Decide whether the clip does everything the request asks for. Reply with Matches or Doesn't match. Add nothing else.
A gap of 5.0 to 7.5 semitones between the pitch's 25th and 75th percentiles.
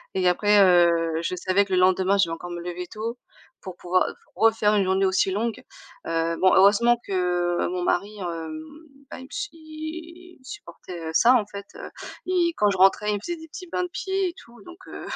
Matches